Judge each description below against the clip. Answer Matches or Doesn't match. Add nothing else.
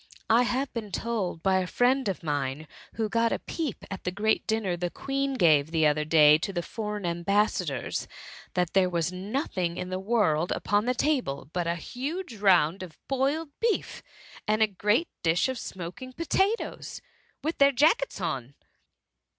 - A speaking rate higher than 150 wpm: Matches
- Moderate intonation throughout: Doesn't match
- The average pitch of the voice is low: Doesn't match